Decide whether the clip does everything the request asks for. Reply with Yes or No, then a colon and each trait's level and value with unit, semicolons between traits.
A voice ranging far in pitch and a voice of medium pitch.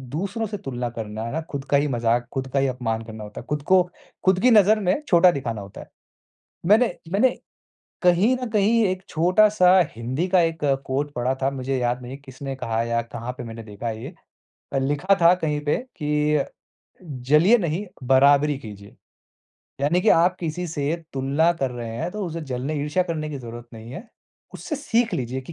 Yes: wide, 6.5 semitones; medium, 145 Hz